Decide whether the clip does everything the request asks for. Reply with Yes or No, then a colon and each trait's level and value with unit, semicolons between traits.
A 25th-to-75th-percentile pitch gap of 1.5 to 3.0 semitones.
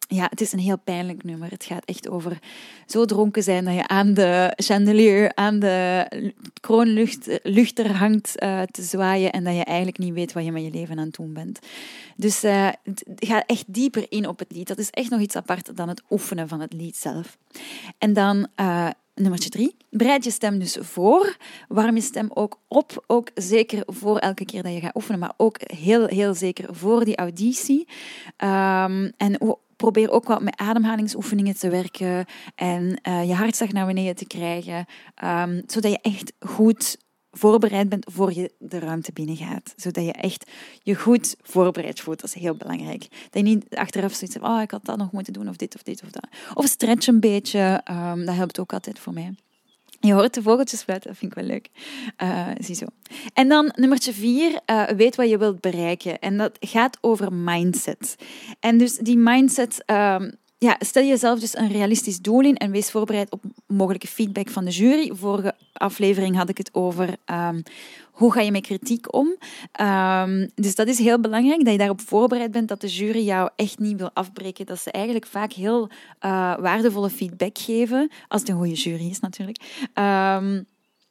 No: average, 3.6 semitones